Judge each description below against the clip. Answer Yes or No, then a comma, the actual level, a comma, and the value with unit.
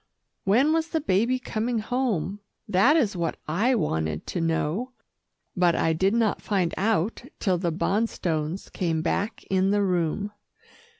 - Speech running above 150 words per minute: No, average, 145 wpm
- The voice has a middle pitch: No, high, 195 Hz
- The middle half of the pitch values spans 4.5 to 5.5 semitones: Yes, average, 5.2 semitones